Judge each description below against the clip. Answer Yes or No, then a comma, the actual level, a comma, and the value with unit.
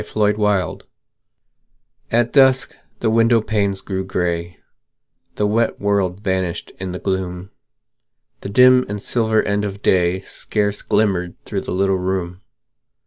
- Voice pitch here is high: No, low, 100 Hz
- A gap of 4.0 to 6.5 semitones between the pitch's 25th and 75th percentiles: No, average, 2.7 semitones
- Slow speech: Yes, slow, 130 wpm